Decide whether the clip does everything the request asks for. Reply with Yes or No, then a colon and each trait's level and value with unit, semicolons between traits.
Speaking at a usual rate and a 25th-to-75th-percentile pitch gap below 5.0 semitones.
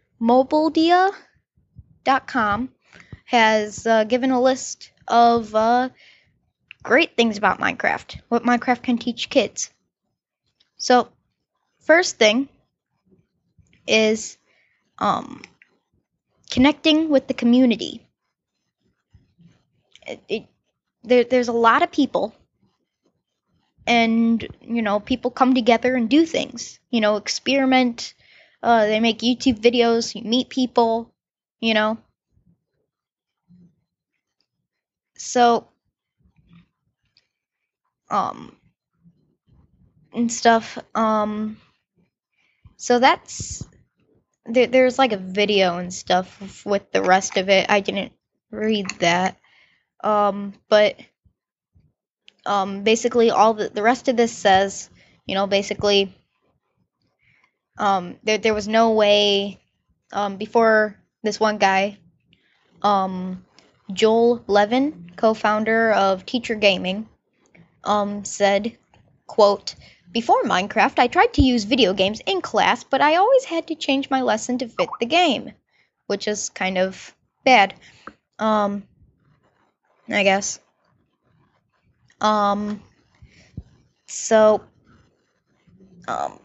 No: slow, 105 wpm; average, 3.6 semitones